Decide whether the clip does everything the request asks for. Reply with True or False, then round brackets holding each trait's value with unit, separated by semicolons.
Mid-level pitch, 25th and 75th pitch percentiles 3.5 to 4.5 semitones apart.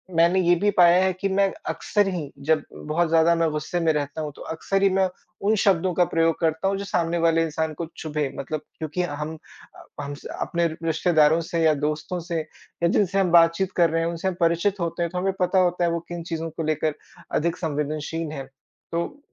False (165 Hz; 2.4 semitones)